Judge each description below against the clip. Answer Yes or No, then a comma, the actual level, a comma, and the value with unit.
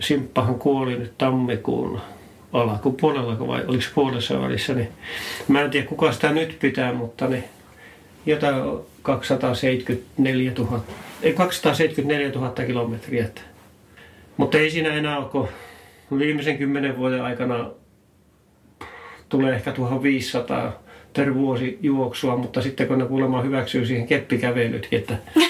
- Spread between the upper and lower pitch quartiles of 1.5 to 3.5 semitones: Yes, average, 2.7 semitones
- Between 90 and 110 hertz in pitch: No, low, 130 Hz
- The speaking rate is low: No, average, 125 wpm